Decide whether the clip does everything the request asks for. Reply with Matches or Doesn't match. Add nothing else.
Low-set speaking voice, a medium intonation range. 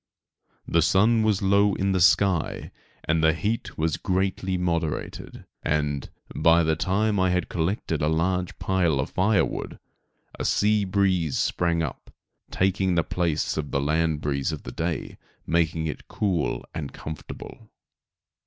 Matches